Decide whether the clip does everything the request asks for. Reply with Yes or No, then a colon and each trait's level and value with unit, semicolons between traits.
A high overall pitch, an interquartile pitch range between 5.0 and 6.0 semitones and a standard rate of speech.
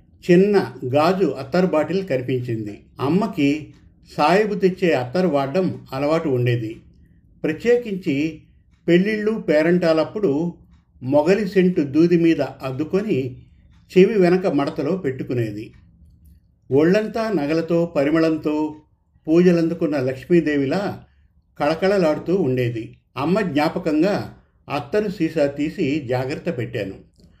No: medium, 155 Hz; wide, 5.6 semitones; average, 85 wpm